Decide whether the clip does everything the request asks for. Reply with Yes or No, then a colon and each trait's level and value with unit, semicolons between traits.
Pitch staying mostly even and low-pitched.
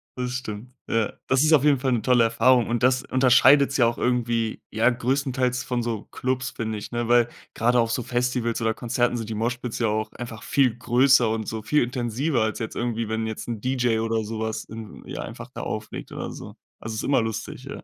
Yes: narrow, 2.2 semitones; low, 120 Hz